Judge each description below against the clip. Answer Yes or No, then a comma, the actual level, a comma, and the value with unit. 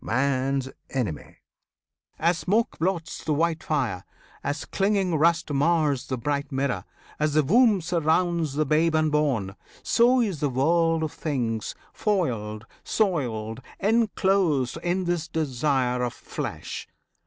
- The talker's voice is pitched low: No, medium, 155 Hz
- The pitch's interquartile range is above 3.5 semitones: Yes, average, 4.6 semitones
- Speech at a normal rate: No, slow, 125 wpm